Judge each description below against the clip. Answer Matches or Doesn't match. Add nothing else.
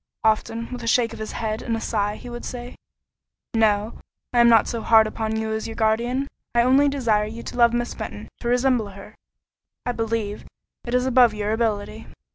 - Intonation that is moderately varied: Doesn't match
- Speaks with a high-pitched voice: Matches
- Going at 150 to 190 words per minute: Doesn't match